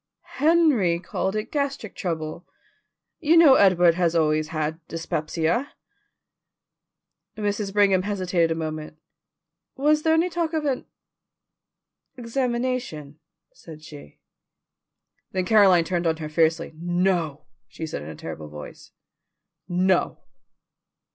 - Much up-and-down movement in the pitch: Yes, wide, 7.0 semitones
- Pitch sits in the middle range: Yes, medium, 180 Hz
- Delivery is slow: Yes, slow, 115 wpm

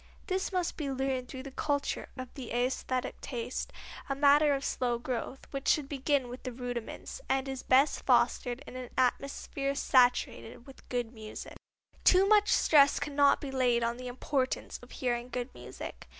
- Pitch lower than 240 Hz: No, very high, 260 Hz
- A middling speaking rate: Yes, average, 170 wpm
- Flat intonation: Yes, narrow, 2.2 semitones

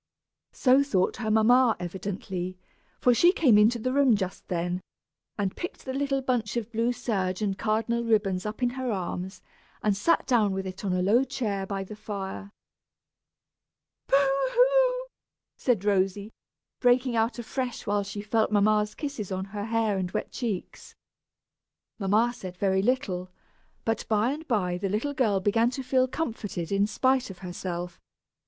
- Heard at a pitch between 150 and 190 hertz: No, high, 215 Hz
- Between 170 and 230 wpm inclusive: No, average, 160 wpm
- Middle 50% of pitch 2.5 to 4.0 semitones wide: No, average, 4.4 semitones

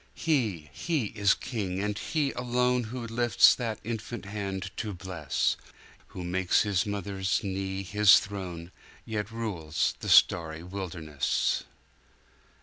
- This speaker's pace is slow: Yes, slow, 120 wpm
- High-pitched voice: No, low, 100 Hz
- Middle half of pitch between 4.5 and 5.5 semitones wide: No, average, 3.7 semitones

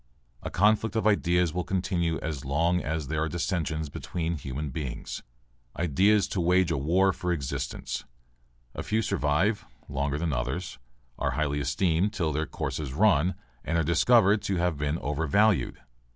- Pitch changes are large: No, average, 4.1 semitones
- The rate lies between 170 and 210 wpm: No, average, 160 wpm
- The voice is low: Yes, very low, 85 Hz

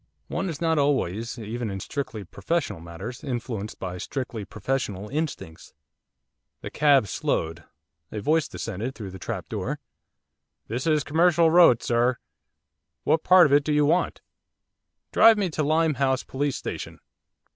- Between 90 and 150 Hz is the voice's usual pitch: Yes, low, 135 Hz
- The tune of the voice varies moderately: No, wide, 6.4 semitones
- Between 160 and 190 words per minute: No, average, 145 wpm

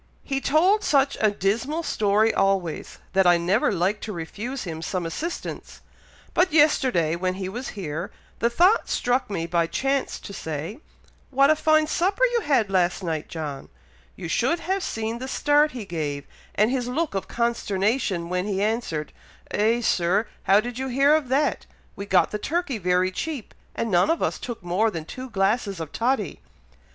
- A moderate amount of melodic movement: No, wide, 6.8 semitones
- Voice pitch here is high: Yes, high, 215 Hz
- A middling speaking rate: Yes, average, 180 wpm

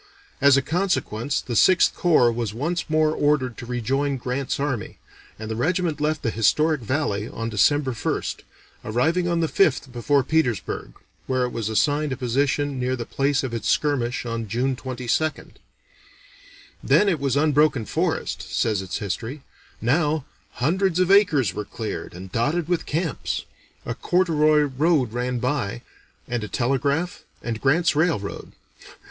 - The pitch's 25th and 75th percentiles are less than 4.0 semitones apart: No, average, 4.6 semitones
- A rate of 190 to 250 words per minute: No, average, 155 wpm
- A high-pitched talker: No, low, 135 Hz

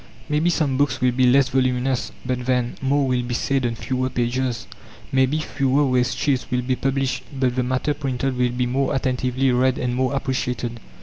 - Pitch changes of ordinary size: No, narrow, 1.4 semitones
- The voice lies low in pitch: Yes, low, 130 Hz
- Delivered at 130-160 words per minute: No, average, 190 wpm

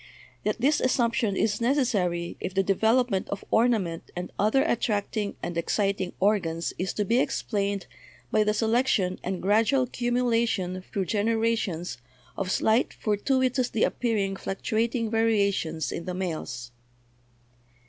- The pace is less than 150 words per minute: Yes, slow, 135 wpm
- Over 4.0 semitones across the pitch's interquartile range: No, average, 3.7 semitones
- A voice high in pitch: Yes, high, 210 Hz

